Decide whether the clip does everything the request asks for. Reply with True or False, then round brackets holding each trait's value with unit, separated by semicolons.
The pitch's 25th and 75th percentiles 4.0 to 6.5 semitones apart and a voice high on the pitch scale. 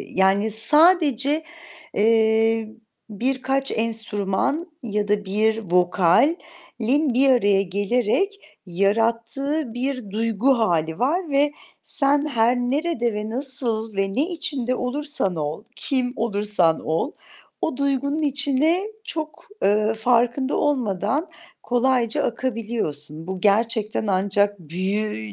True (5.2 semitones; 230 Hz)